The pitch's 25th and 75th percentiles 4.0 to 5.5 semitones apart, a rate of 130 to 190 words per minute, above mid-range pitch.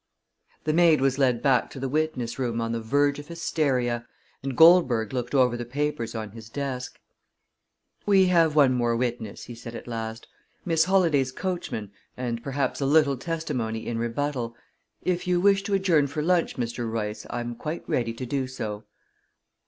No: average, 4.8 semitones; average, 175 wpm; low, 130 Hz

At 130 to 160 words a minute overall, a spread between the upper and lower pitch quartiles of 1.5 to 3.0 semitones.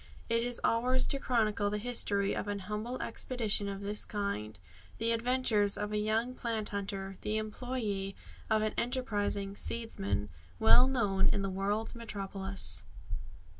Yes: average, 145 wpm; average, 2.7 semitones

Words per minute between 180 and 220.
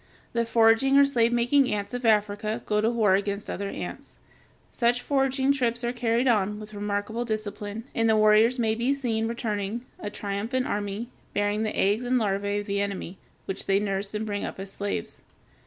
Yes: average, 190 wpm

